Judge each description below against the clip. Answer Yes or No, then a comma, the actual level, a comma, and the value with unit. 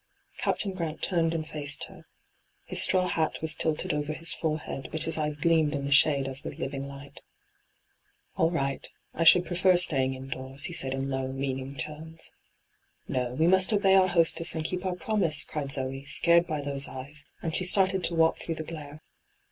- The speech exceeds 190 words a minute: Yes, fast, 205 wpm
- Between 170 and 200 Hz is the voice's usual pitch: No, medium, 155 Hz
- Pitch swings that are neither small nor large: Yes, average, 3.6 semitones